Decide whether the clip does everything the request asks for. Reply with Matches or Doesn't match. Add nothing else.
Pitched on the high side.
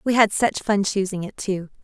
Matches